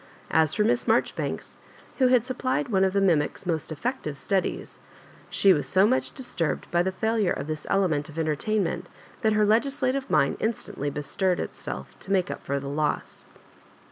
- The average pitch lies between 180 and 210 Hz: Yes, high, 190 Hz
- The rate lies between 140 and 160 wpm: No, average, 180 wpm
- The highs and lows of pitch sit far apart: Yes, wide, 6.4 semitones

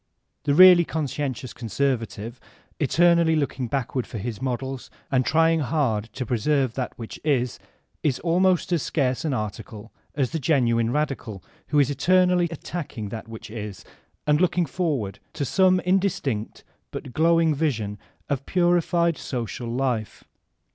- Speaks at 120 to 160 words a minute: Yes, average, 145 wpm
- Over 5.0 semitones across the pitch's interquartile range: Yes, wide, 5.6 semitones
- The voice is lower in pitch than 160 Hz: Yes, medium, 140 Hz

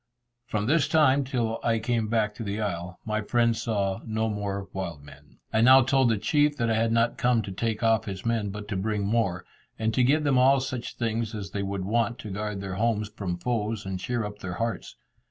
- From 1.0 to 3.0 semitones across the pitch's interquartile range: Yes, average, 2.7 semitones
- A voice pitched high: No, low, 110 Hz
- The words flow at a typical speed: No, fast, 225 wpm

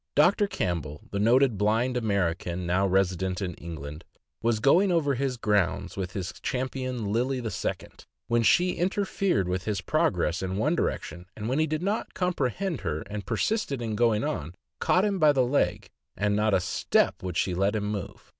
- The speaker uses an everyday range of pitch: No, wide, 6.7 semitones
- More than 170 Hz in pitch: No, low, 105 Hz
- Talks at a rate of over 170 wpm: Yes, average, 185 wpm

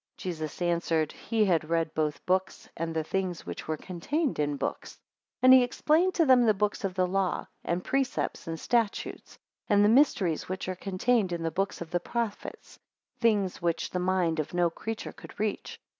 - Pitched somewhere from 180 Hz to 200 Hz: Yes, medium, 185 Hz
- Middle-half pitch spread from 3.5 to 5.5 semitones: Yes, average, 4.8 semitones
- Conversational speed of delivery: Yes, average, 195 wpm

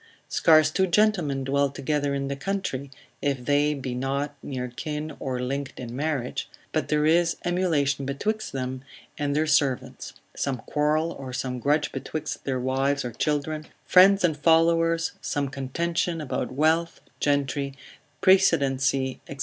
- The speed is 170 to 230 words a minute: No, average, 145 wpm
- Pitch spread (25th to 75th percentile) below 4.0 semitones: Yes, average, 3.0 semitones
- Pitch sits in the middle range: Yes, medium, 145 Hz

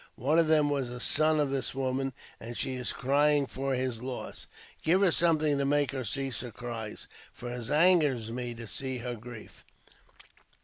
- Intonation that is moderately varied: Yes, average, 3.2 semitones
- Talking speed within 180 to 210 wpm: Yes, average, 185 wpm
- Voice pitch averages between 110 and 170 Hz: Yes, low, 135 Hz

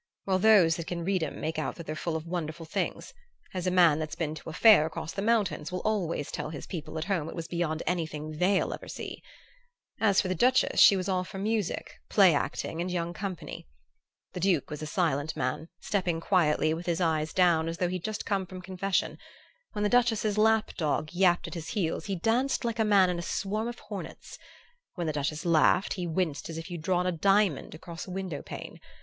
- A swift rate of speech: Yes, fast, 220 wpm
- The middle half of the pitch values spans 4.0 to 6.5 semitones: No, average, 3.5 semitones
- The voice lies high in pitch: No, medium, 175 Hz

